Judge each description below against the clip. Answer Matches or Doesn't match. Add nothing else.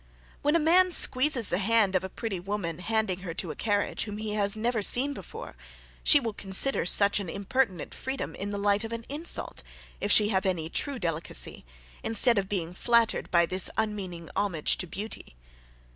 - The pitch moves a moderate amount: Matches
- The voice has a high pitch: Matches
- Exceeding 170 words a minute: Matches